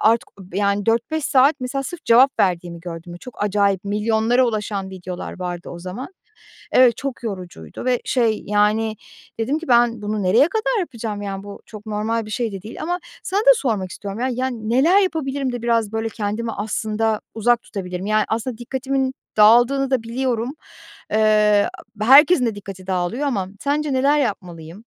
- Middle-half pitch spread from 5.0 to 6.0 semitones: No, average, 4.1 semitones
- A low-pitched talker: No, high, 225 Hz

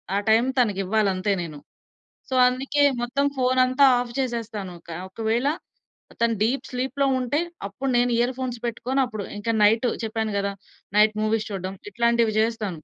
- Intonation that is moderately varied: Yes, average, 3.2 semitones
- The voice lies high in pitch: Yes, high, 230 Hz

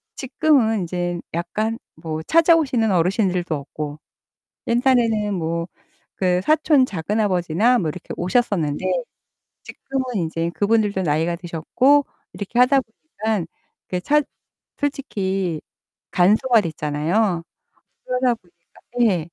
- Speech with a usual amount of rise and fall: No, wide, 6.2 semitones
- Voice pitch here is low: No, high, 195 Hz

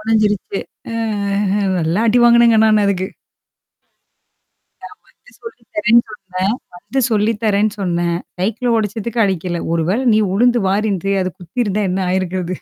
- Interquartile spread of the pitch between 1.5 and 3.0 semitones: No, average, 3.4 semitones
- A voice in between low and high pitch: No, high, 210 Hz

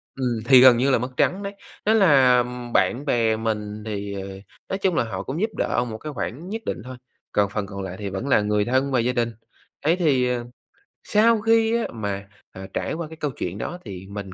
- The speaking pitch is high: No, low, 125 Hz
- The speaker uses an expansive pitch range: Yes, wide, 6.8 semitones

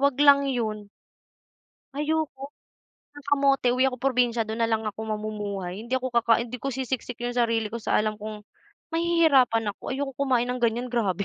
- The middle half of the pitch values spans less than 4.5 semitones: Yes, average, 3.6 semitones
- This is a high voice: Yes, high, 240 Hz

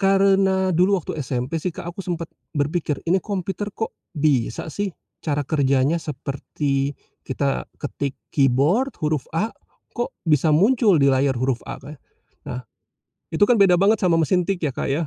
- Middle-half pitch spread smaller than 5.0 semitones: No, wide, 5.5 semitones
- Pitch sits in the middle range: Yes, medium, 160 Hz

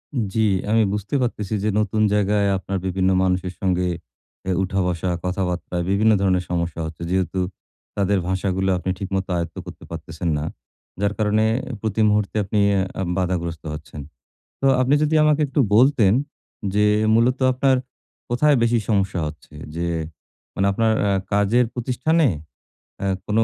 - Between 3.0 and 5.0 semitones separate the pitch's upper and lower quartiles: Yes, average, 3.5 semitones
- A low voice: Yes, low, 100 Hz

